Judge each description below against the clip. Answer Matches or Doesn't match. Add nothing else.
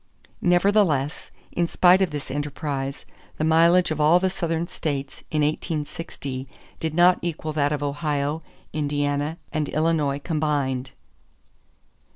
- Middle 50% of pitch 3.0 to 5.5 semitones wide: Doesn't match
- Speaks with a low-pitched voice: Doesn't match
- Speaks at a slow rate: Matches